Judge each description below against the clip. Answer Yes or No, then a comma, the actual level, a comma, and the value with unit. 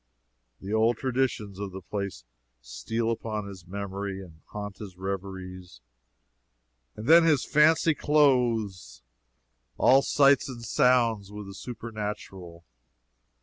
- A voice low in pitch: Yes, low, 105 Hz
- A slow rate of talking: Yes, slow, 115 wpm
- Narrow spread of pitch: No, average, 4.1 semitones